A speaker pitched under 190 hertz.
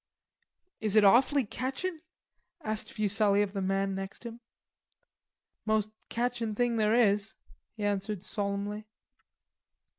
No: high, 215 Hz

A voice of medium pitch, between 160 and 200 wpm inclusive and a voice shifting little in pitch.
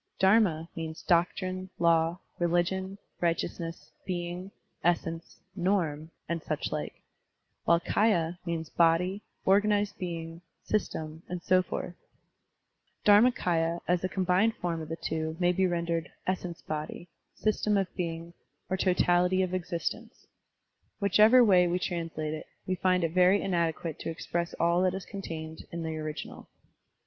No: medium, 175 Hz; average, 140 wpm; narrow, 2.2 semitones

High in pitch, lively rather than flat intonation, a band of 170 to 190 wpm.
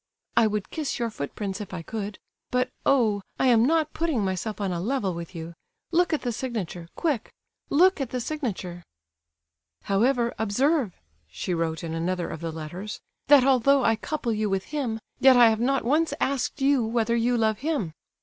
Yes: high, 225 Hz; wide, 6.1 semitones; average, 180 wpm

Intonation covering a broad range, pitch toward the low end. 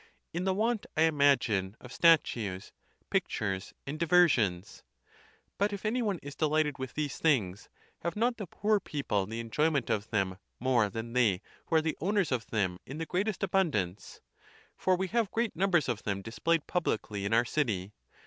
No: wide, 8.8 semitones; medium, 145 Hz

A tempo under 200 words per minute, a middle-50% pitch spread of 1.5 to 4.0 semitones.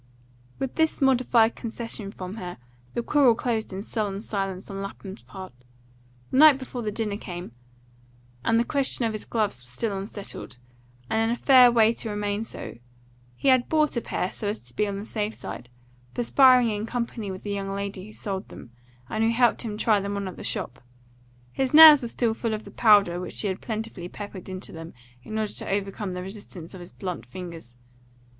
No: fast, 205 wpm; average, 3.4 semitones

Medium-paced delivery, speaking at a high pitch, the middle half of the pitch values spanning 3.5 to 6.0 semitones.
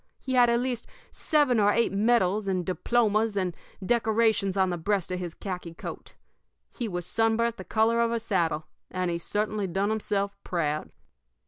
Yes: average, 175 wpm; high, 205 Hz; average, 4.0 semitones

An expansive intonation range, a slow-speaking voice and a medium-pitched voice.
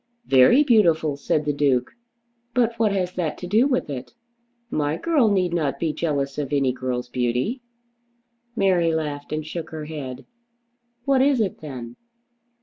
No: wide, 6.2 semitones; average, 155 wpm; medium, 155 Hz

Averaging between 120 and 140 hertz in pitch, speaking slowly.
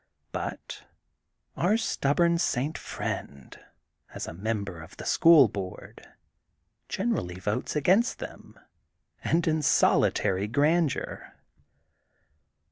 Yes: low, 135 Hz; slow, 95 wpm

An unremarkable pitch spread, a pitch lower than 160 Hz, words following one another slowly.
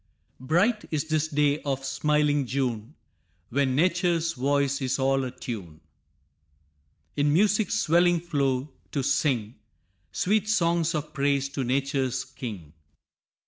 Yes: average, 3.8 semitones; medium, 140 Hz; slow, 115 wpm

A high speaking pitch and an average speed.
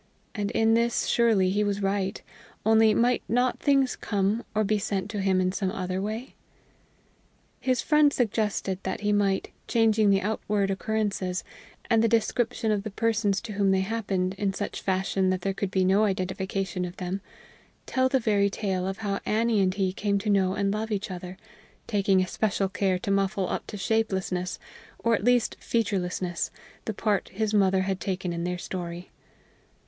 Yes: high, 200 Hz; average, 180 wpm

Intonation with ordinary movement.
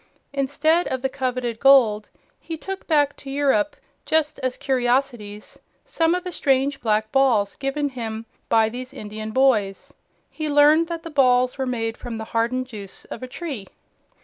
Yes: average, 4.2 semitones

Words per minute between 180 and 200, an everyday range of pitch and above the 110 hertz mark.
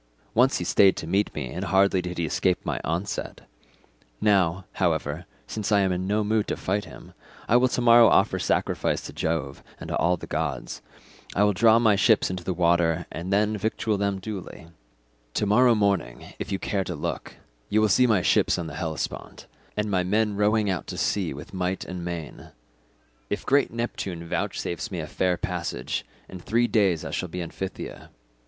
No: average, 195 wpm; average, 3.4 semitones; very low, 95 Hz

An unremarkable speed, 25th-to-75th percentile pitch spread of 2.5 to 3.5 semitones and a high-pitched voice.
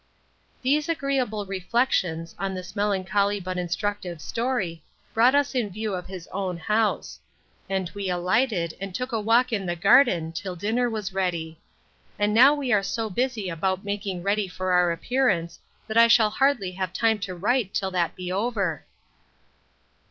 No: average, 165 wpm; average, 4.1 semitones; high, 200 Hz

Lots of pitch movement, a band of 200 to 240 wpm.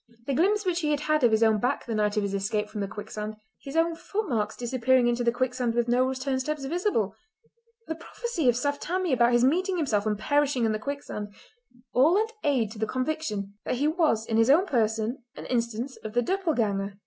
Yes: wide, 6.0 semitones; fast, 205 wpm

